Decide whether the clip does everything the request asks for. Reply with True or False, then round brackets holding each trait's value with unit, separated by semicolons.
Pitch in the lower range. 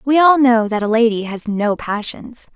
False (230 Hz)